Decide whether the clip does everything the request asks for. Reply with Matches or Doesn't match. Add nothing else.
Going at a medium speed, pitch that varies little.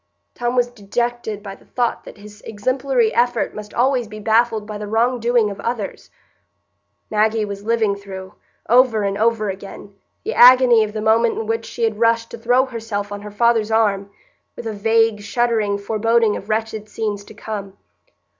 Matches